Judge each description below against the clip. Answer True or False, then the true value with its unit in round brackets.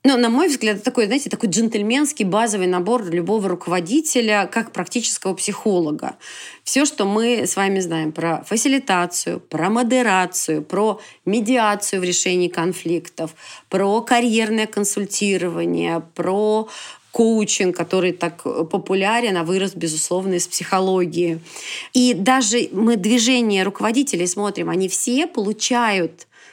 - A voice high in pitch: True (200 Hz)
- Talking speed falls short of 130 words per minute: True (120 wpm)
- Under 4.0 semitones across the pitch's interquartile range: False (4.5 semitones)